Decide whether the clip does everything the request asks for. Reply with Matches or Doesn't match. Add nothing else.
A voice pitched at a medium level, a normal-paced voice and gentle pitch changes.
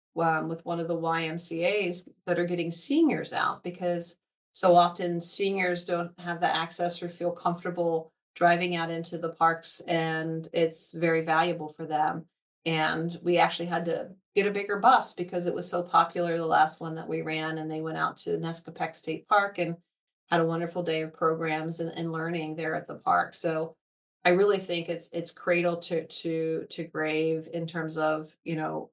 Matches